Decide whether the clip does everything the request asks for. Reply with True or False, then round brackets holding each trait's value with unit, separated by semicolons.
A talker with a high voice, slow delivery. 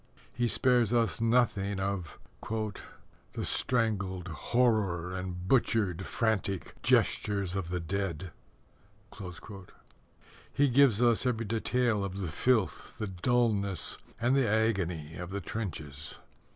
False (100 Hz; 110 wpm)